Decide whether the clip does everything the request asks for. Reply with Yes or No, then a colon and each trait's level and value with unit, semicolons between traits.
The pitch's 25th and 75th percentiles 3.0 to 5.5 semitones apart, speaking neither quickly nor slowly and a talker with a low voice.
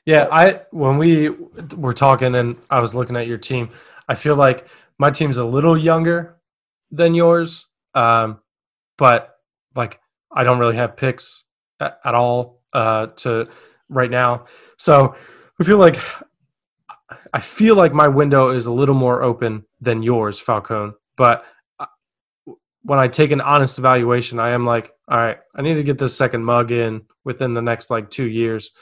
Yes: average, 4.1 semitones; average, 170 wpm; low, 125 Hz